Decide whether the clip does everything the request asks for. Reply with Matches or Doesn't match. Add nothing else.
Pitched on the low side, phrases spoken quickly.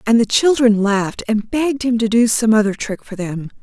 Doesn't match